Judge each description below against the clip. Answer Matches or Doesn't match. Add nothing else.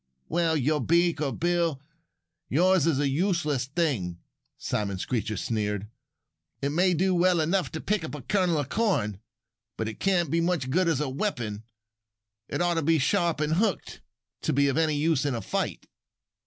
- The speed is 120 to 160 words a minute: Doesn't match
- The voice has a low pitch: Doesn't match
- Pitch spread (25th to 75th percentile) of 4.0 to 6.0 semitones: Matches